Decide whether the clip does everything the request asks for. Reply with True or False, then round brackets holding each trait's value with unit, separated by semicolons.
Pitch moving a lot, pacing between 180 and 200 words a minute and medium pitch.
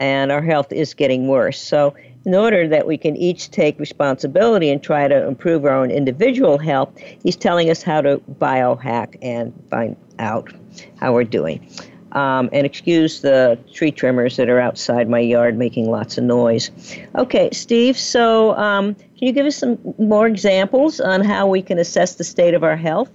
True (6.8 semitones; 185 wpm; 155 Hz)